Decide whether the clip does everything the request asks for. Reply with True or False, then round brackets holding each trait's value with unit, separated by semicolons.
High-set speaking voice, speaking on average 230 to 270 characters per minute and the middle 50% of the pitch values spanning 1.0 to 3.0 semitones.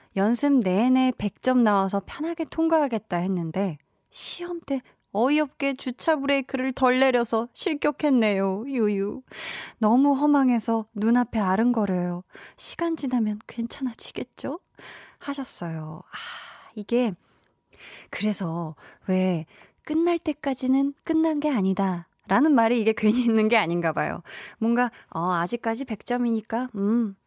False (235 Hz; 265 characters per minute; 5.5 semitones)